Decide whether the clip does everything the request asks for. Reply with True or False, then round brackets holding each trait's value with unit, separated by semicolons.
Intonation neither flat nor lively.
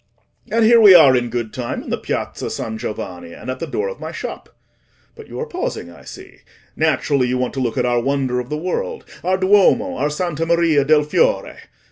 False (8.2 semitones)